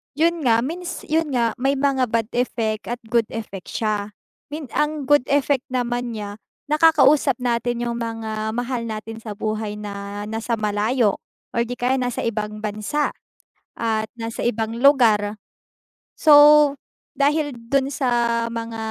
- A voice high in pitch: Yes, high, 235 Hz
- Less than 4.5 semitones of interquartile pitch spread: Yes, average, 4.1 semitones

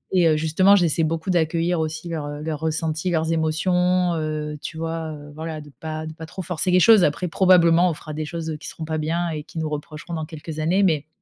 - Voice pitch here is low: No, medium, 160 Hz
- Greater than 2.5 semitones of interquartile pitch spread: No, narrow, 1.9 semitones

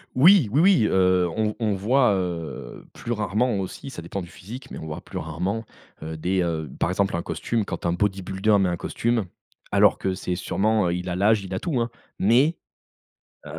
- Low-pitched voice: Yes, very low, 95 Hz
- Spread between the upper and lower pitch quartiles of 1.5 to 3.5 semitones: No, average, 4.1 semitones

